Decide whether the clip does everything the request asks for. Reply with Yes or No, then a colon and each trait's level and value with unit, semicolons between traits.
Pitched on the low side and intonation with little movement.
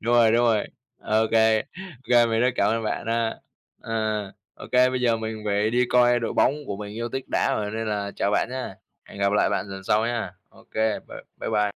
Yes: low, 110 Hz; narrow, 2.0 semitones